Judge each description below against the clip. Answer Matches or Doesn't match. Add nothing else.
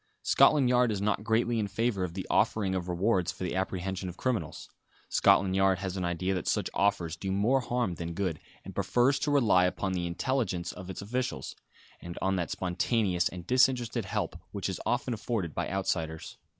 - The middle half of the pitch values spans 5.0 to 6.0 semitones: Doesn't match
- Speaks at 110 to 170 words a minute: Doesn't match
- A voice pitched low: Matches